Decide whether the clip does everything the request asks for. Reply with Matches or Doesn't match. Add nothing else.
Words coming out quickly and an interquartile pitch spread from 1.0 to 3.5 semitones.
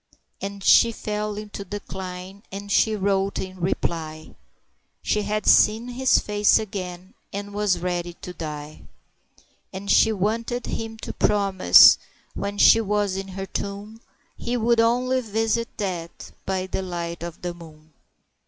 Doesn't match